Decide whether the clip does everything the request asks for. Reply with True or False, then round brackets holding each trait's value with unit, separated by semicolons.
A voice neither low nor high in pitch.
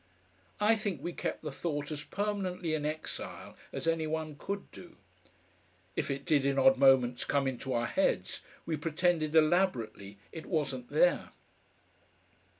True (155 Hz)